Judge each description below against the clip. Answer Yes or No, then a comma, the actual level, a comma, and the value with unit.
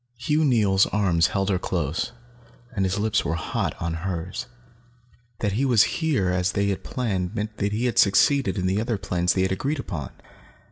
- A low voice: Yes, low, 100 Hz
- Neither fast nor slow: Yes, average, 190 wpm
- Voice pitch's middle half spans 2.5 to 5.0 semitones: Yes, average, 3.9 semitones